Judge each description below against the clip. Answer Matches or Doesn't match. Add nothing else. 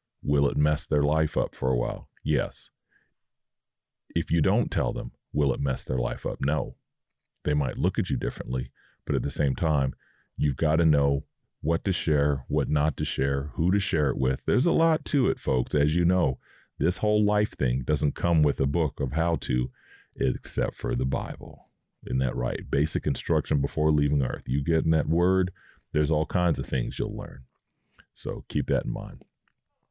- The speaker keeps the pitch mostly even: Doesn't match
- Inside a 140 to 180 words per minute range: Doesn't match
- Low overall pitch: Matches